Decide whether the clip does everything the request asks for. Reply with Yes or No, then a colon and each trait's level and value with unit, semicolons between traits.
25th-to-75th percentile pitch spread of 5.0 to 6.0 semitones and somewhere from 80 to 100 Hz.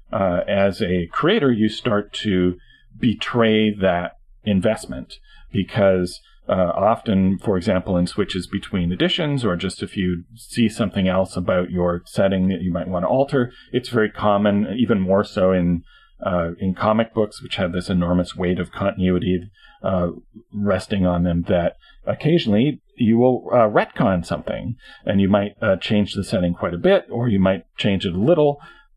No: average, 3.3 semitones; very low, 95 Hz